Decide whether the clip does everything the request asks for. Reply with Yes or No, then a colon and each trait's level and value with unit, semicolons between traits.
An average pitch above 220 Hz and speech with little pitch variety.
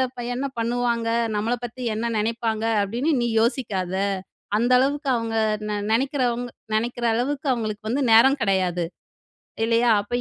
Yes: high, 235 Hz; narrow, 2.1 semitones